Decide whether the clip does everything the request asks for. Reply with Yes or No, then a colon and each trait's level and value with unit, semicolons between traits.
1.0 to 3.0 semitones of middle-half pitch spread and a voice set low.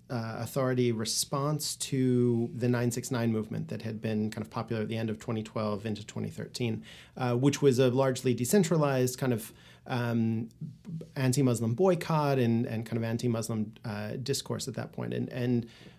Yes: average, 2.7 semitones; low, 120 Hz